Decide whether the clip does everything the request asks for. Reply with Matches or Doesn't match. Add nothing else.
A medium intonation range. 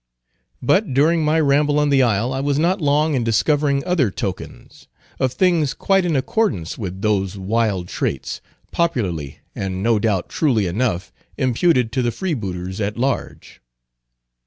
Doesn't match